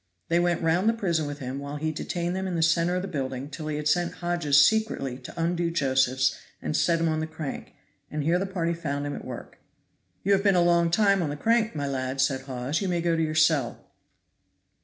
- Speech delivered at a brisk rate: Yes, fast, 240 wpm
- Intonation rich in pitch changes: No, average, 3.5 semitones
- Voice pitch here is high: No, medium, 160 Hz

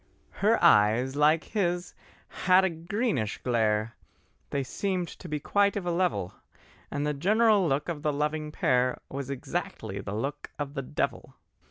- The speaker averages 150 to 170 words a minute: Yes, average, 160 wpm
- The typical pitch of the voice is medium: Yes, medium, 150 Hz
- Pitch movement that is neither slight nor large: No, wide, 5.7 semitones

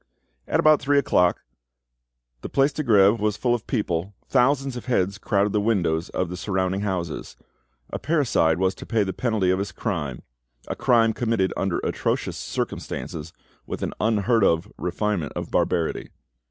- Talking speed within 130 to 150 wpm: No, average, 160 wpm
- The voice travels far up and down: No, average, 4.5 semitones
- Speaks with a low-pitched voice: Yes, low, 100 Hz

